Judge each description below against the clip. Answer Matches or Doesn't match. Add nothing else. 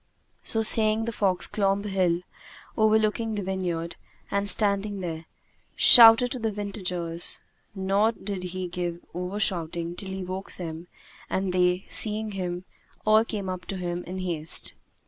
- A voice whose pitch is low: Doesn't match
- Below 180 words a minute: Matches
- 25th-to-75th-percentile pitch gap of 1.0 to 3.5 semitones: Matches